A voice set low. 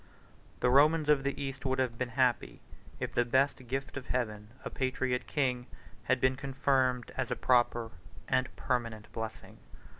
Yes: low, 130 Hz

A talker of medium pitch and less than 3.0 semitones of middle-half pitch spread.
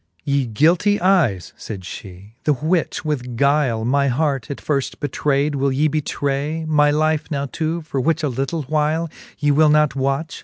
Yes: medium, 145 Hz; narrow, 2.4 semitones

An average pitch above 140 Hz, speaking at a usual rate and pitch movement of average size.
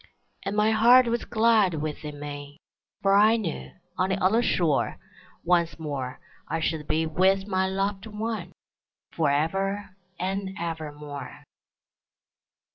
No: high, 190 Hz; slow, 120 wpm; average, 5.0 semitones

